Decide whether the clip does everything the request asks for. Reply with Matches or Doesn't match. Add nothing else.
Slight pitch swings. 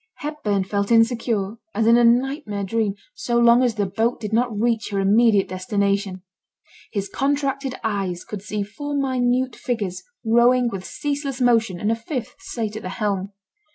Doesn't match